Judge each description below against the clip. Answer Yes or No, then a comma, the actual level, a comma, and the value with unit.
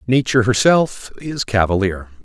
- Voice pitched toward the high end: No, low, 115 Hz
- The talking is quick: No, slow, 105 wpm